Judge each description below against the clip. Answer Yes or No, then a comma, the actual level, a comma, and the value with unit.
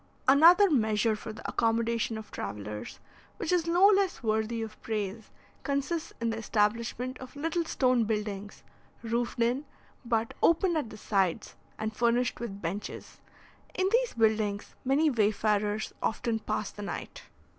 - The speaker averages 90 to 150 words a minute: Yes, average, 145 wpm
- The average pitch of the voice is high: Yes, high, 230 Hz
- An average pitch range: Yes, average, 4.4 semitones